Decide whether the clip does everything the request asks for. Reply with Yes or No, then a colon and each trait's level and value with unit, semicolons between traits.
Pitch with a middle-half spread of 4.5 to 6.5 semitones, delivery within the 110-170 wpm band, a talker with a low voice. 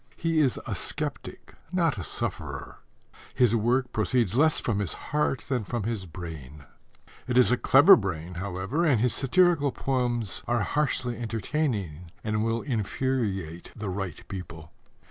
Yes: wide, 5.6 semitones; average, 145 wpm; low, 115 Hz